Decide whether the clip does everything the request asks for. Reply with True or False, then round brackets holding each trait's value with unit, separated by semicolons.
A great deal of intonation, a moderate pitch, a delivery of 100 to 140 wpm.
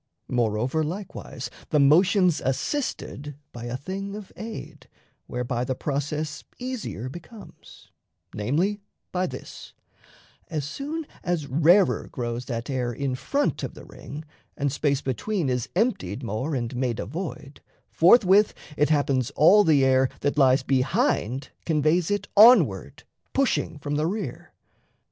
True (6.4 semitones; 150 Hz; 135 wpm)